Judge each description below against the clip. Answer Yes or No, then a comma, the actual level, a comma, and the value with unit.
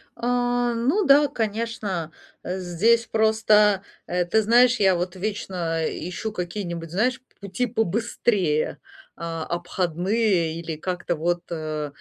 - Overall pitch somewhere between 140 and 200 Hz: Yes, high, 190 Hz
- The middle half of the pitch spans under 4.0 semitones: No, average, 4.9 semitones